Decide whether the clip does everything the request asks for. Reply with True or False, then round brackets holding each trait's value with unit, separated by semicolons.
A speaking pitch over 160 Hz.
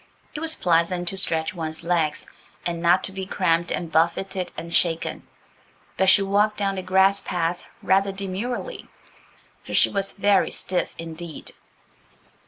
True (185 Hz)